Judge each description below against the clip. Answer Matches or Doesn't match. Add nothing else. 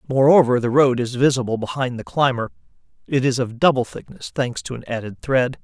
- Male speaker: Matches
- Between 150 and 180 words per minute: Doesn't match